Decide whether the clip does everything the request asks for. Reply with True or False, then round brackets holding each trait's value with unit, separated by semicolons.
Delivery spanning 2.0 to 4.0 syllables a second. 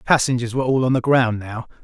False (7.2 syllables/s)